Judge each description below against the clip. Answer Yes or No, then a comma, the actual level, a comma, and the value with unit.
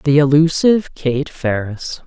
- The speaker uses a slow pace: Yes, slow, 115 wpm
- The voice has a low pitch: No, medium, 145 Hz